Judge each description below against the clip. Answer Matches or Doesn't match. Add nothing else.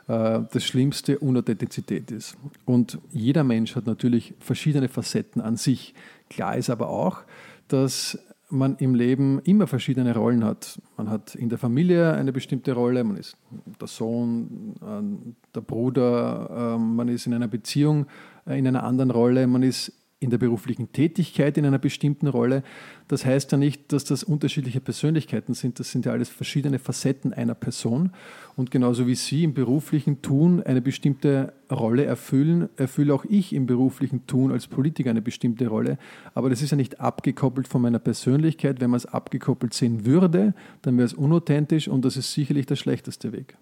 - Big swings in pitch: Doesn't match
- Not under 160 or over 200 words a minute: Matches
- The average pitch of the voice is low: Matches